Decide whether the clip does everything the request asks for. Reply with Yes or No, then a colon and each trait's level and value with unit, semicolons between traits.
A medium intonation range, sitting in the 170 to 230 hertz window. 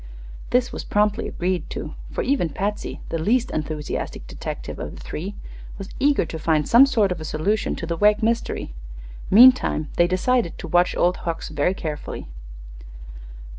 No: wide, 5.7 semitones; medium, 185 Hz